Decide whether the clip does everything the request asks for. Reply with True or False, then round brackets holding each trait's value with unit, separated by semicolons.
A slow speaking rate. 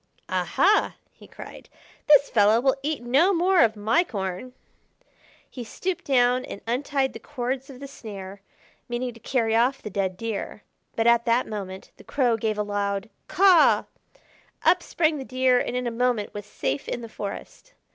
False (175 wpm)